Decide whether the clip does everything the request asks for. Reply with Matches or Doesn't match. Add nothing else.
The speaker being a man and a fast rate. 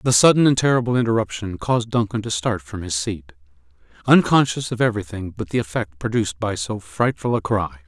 Doesn't match